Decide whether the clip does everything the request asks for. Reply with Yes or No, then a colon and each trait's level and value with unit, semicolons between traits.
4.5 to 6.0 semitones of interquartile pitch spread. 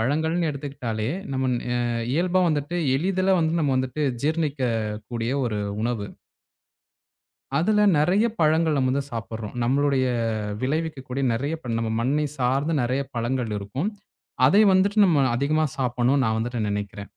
Yes: average, 4.9 semitones